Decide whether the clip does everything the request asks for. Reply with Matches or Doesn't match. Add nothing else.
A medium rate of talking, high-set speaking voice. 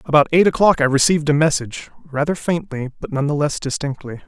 Doesn't match